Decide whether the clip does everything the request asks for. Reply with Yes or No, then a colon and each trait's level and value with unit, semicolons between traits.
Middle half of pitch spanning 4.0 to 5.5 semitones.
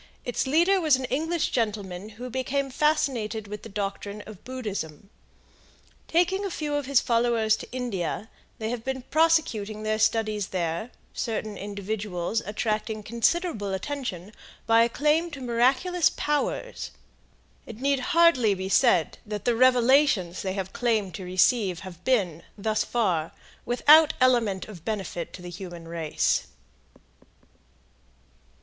Yes: average, 5.0 semitones